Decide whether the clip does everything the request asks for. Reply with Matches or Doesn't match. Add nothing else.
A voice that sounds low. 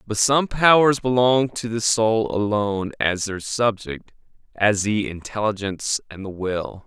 Matches